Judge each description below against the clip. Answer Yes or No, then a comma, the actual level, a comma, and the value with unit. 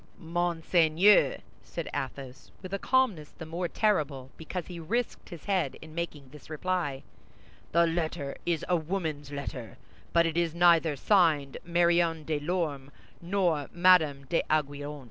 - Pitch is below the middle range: No, medium, 165 Hz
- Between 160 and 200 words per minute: No, average, 140 wpm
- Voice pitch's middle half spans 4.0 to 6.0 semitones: No, average, 3.1 semitones